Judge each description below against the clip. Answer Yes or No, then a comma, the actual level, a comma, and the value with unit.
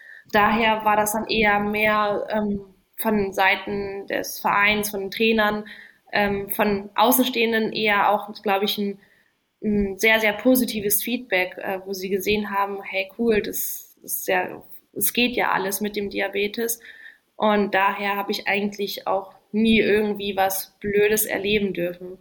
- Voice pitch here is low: No, high, 205 Hz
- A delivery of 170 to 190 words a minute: No, average, 150 wpm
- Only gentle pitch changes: Yes, narrow, 1.4 semitones